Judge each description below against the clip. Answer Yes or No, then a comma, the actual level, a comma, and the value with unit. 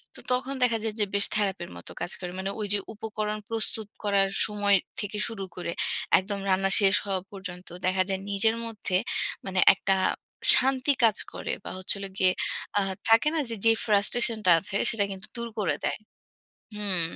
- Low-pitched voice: No, high, 205 Hz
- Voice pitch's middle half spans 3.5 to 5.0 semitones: No, narrow, 2.5 semitones